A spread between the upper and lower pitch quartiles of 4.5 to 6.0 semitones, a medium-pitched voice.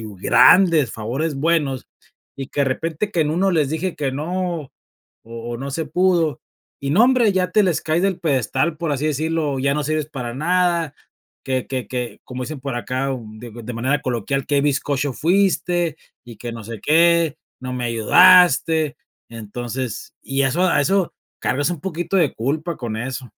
Yes: average, 4.8 semitones; medium, 145 Hz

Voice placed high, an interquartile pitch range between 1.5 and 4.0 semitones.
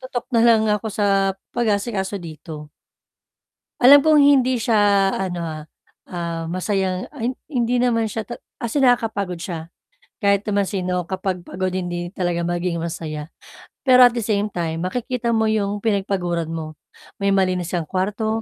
No: high, 195 Hz; average, 4.4 semitones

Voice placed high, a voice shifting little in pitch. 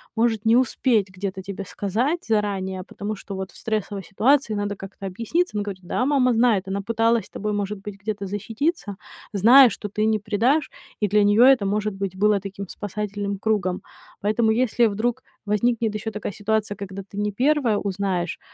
Yes: high, 210 Hz; narrow, 2.3 semitones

